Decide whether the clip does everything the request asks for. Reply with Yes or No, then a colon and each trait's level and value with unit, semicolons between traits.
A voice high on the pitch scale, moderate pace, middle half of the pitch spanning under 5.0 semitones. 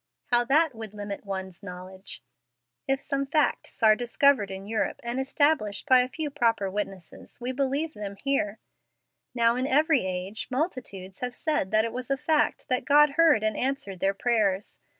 No: high, 240 Hz; average, 170 wpm; wide, 5.5 semitones